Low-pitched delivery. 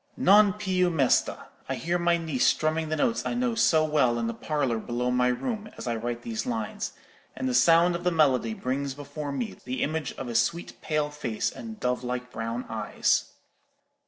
No: medium, 145 Hz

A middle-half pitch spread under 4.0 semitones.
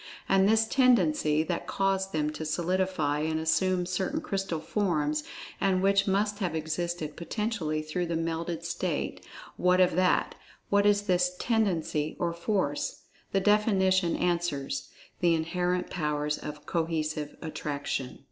Yes: average, 3.6 semitones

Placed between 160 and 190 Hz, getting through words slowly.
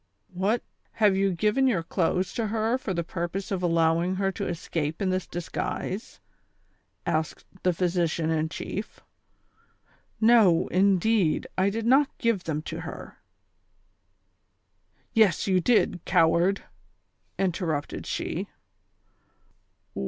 Yes: medium, 185 Hz; slow, 130 wpm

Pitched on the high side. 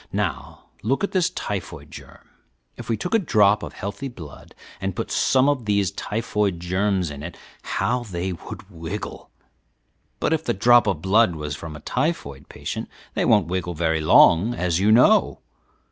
No: low, 100 Hz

